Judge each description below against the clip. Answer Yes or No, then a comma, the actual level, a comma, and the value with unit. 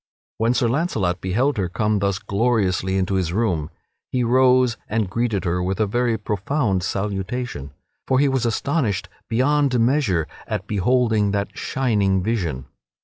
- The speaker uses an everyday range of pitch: Yes, average, 4.6 semitones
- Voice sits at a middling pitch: No, low, 110 Hz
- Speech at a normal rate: Yes, average, 145 wpm